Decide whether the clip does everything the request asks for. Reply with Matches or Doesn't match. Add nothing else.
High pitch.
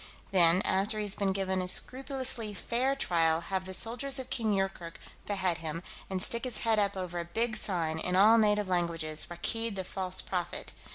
Matches